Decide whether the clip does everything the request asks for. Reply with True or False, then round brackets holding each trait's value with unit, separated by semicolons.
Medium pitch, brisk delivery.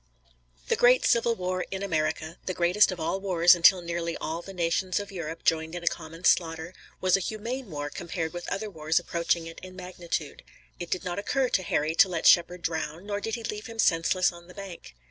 True (175 Hz; 215 wpm)